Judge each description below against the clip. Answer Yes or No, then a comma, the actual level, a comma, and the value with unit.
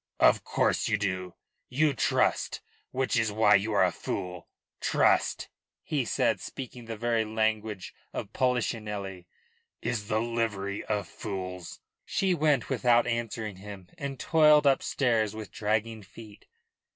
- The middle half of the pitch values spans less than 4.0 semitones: Yes, average, 3.1 semitones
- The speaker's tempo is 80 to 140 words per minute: Yes, slow, 135 wpm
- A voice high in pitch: No, low, 110 Hz